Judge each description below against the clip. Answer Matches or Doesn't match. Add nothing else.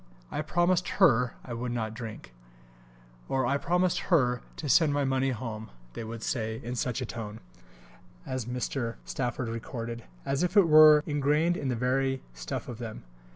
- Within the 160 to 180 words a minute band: Matches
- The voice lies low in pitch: Matches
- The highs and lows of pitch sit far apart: Doesn't match